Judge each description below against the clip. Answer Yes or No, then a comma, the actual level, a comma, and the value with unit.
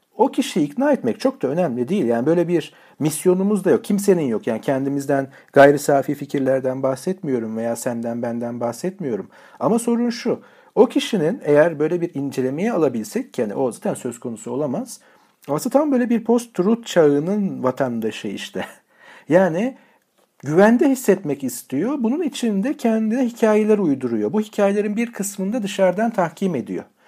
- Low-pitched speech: No, medium, 185 Hz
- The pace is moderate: No, fast, 150 wpm